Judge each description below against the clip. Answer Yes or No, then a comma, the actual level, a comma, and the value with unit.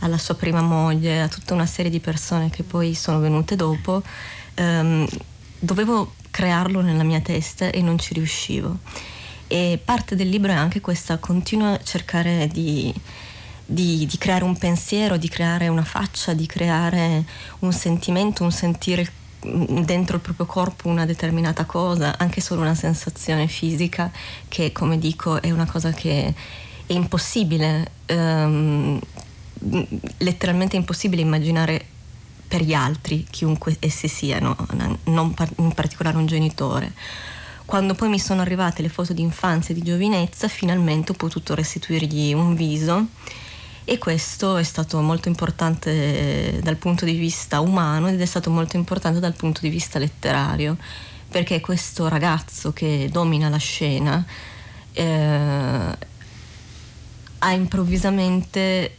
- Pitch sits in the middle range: Yes, medium, 165 Hz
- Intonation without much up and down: Yes, narrow, 2.2 semitones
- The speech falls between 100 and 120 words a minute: No, average, 135 wpm